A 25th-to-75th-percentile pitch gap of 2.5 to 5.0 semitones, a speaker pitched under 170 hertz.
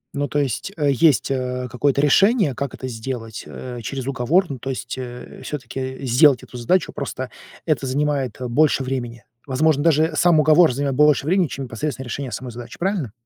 Yes: average, 3.0 semitones; low, 135 Hz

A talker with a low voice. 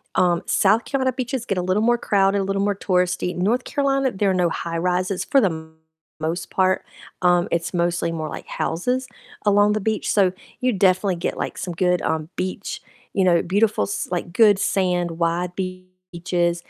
No: medium, 185 Hz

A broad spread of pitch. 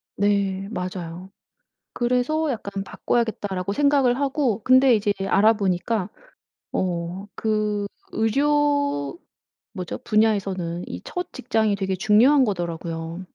No: average, 5.0 semitones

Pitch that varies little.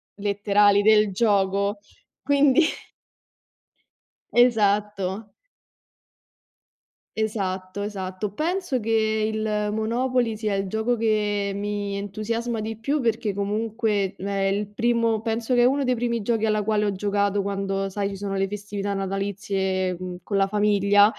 Yes: narrow, 2.0 semitones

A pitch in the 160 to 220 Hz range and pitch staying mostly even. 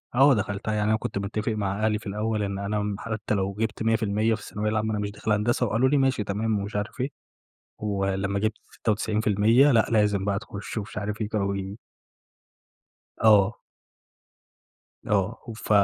No: low, 105 Hz; narrow, 1.6 semitones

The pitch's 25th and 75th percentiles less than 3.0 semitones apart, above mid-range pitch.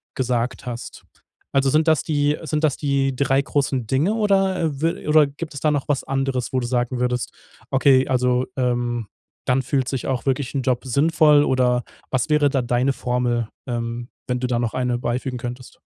No: narrow, 2.6 semitones; low, 130 Hz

